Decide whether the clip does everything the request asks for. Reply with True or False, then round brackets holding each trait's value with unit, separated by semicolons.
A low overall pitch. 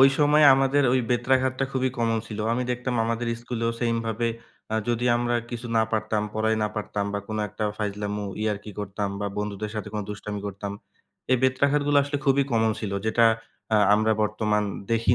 True (115 Hz)